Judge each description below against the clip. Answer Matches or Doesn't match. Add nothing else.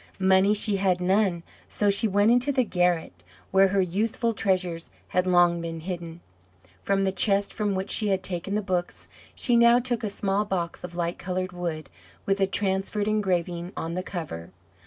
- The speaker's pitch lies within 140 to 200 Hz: Matches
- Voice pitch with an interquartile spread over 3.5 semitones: Doesn't match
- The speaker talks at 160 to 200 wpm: Matches